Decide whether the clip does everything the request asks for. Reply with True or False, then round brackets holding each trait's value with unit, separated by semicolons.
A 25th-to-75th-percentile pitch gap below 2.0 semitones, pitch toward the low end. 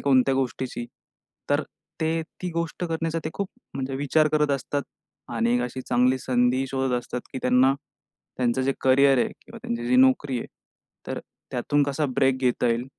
False (2.6 semitones; 130 Hz)